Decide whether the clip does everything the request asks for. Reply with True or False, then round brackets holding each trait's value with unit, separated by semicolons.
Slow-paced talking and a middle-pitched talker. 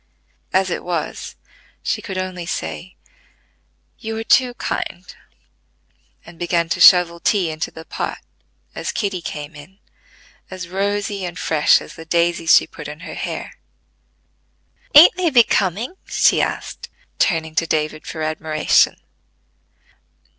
True (130 wpm; 175 Hz)